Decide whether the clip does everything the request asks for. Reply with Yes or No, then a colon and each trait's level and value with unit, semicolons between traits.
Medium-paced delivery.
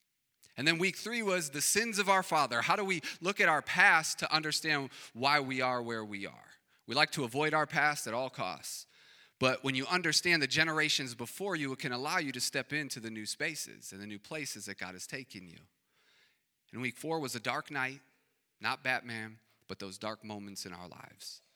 No: fast, 215 wpm